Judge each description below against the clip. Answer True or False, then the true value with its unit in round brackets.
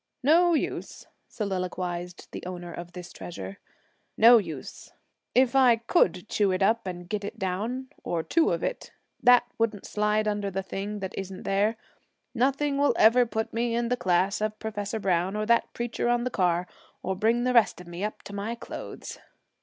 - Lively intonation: False (4.3 semitones)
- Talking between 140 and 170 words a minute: False (185 wpm)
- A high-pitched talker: True (210 Hz)